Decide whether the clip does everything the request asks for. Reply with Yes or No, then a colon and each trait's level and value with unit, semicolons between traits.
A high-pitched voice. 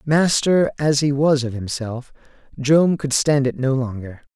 No: low, 135 Hz